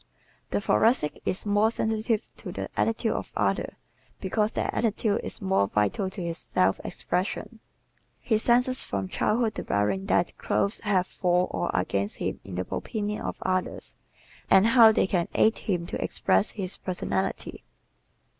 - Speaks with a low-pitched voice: No, high, 195 Hz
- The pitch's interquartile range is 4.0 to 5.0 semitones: Yes, average, 4.3 semitones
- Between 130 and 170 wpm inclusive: Yes, average, 155 wpm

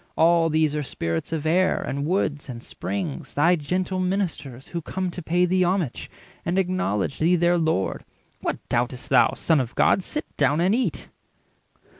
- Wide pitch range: No, average, 4.3 semitones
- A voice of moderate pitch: Yes, medium, 165 Hz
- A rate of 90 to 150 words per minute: No, average, 170 wpm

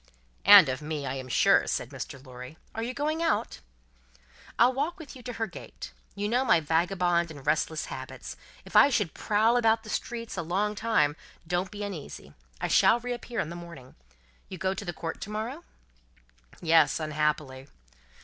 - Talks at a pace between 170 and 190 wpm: Yes, average, 180 wpm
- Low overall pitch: No, medium, 185 Hz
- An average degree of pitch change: No, wide, 6.8 semitones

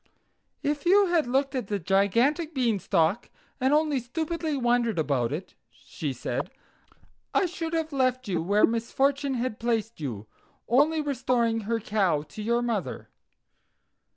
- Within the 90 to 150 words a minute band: Yes, average, 140 wpm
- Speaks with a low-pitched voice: No, high, 240 Hz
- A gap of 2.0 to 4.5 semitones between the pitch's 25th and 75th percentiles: No, wide, 5.5 semitones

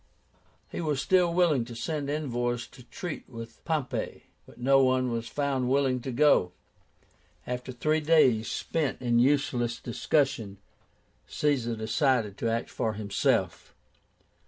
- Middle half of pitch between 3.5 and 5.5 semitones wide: Yes, average, 3.8 semitones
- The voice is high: No, low, 130 Hz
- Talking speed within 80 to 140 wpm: Yes, slow, 135 wpm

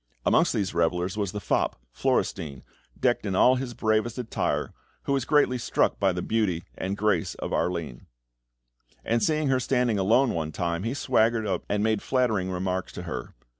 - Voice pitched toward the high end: No, low, 105 Hz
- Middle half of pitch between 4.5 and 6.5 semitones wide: Yes, average, 5.1 semitones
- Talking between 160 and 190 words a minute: Yes, average, 175 wpm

